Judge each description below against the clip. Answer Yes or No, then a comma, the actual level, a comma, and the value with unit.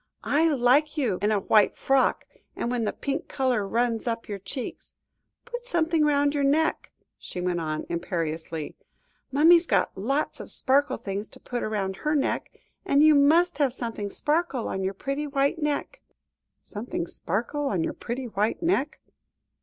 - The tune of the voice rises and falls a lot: Yes, wide, 6.4 semitones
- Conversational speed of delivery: Yes, average, 165 wpm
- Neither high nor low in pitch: No, very high, 260 Hz